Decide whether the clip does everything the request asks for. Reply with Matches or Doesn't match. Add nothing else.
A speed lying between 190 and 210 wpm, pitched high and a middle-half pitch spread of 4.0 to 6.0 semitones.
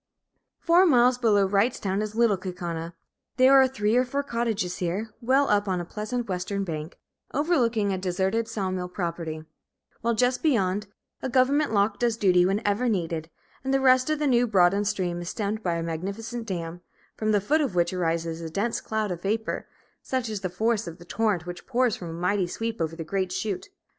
Matches